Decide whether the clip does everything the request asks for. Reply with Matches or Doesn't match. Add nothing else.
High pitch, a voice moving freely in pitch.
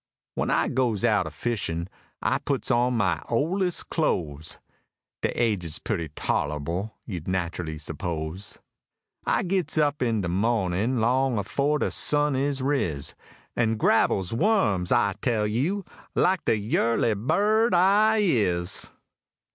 Doesn't match